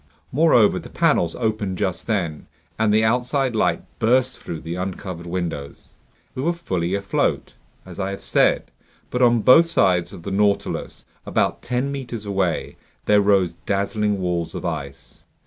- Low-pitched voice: Yes, low, 100 Hz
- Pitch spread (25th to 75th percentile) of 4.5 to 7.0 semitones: Yes, average, 5.1 semitones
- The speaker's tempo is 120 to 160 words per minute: Yes, average, 155 wpm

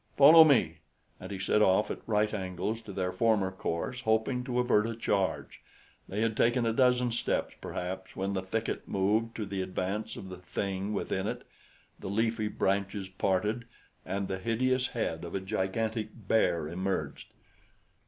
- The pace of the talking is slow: No, average, 165 wpm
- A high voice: No, low, 105 Hz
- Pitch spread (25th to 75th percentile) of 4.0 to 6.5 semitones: No, average, 3.3 semitones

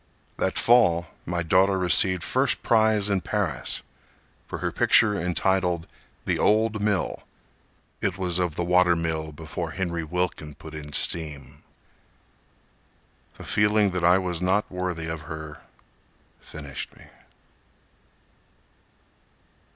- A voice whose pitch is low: Yes, very low, 90 Hz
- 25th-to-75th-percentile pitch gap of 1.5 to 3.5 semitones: Yes, average, 2.9 semitones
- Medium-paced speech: No, slow, 120 wpm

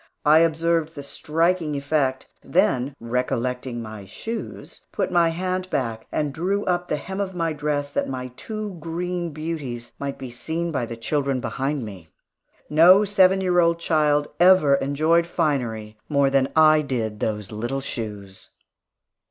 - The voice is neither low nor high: Yes, medium, 150 Hz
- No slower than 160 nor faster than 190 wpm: No, average, 150 wpm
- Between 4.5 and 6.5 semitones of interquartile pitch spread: Yes, average, 5.0 semitones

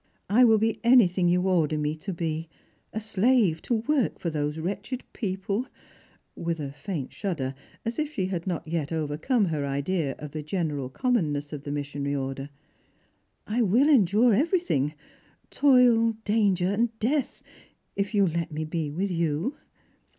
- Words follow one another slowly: No, average, 165 wpm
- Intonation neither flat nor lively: No, wide, 6.6 semitones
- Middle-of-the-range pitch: Yes, medium, 180 Hz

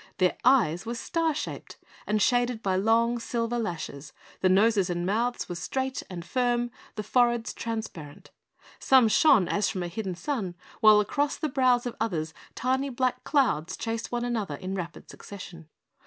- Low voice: No, high, 225 Hz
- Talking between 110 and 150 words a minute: No, average, 165 wpm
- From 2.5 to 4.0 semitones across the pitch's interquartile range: No, average, 4.8 semitones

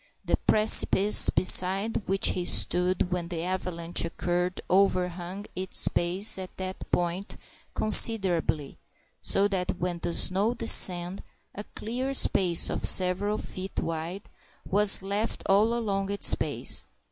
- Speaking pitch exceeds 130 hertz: Yes, medium, 185 Hz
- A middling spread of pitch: No, narrow, 2.2 semitones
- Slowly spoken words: Yes, slow, 125 wpm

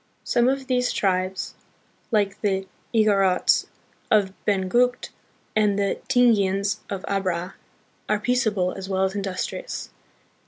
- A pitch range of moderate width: Yes, average, 3.1 semitones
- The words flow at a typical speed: No, slow, 115 wpm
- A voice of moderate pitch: No, high, 200 Hz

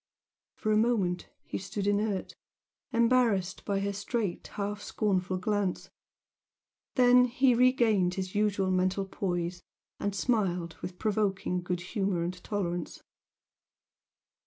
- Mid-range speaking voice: No, high, 200 Hz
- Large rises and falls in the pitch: No, average, 2.9 semitones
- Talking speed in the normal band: No, slow, 115 wpm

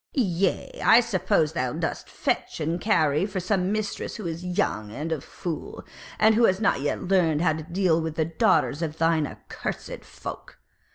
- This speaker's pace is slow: No, average, 180 wpm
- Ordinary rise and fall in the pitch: Yes, average, 3.5 semitones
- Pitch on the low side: No, medium, 170 Hz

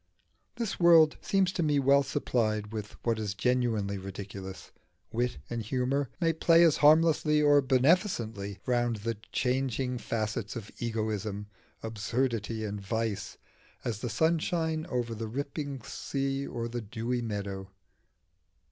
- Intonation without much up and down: No, average, 4.8 semitones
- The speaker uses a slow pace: Yes, slow, 130 wpm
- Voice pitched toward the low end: Yes, low, 120 Hz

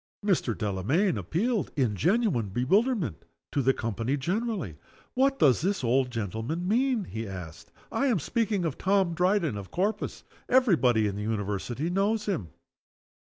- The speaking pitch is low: No, medium, 155 Hz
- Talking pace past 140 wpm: Yes, average, 150 wpm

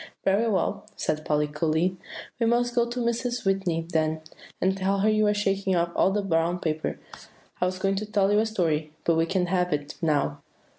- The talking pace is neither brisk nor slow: No, fast, 210 wpm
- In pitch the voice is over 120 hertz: Yes, high, 190 Hz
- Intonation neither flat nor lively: Yes, average, 4.2 semitones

